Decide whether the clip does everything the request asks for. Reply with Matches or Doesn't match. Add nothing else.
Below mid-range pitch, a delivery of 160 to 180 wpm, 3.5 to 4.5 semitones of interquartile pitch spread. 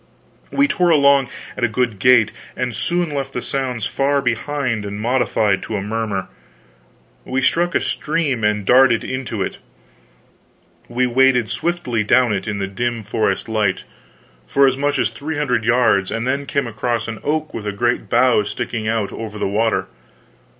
Matches